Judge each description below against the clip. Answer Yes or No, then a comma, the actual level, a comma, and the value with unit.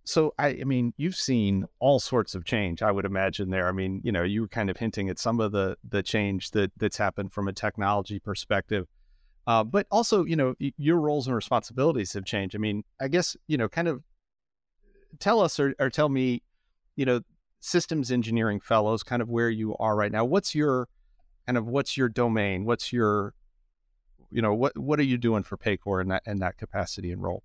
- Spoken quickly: Yes, fast, 215 wpm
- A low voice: Yes, low, 110 Hz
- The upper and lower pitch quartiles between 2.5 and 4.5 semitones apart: No, average, 5.2 semitones